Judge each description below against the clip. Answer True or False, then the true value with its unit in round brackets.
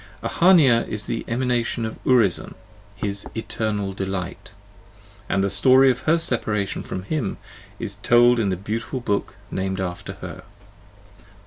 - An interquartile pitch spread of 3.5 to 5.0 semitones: True (3.9 semitones)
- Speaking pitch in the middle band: False (110 Hz)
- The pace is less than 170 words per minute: True (140 wpm)